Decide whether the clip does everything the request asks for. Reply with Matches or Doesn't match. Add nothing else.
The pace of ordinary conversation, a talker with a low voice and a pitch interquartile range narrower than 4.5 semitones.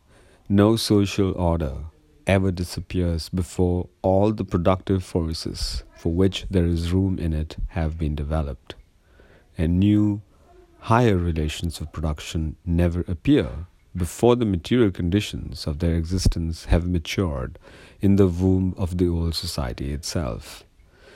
Doesn't match